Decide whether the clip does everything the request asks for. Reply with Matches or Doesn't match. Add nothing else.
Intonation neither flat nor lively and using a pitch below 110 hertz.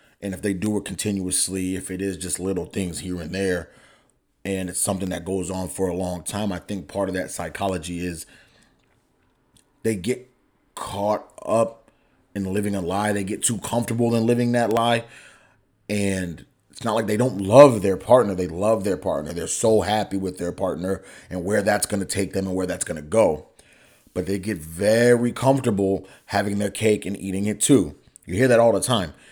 Matches